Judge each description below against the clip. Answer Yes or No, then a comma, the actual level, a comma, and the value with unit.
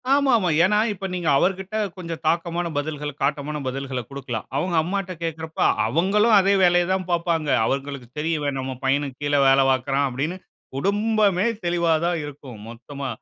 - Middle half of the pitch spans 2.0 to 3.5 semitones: No, average, 4.8 semitones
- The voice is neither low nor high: Yes, medium, 160 Hz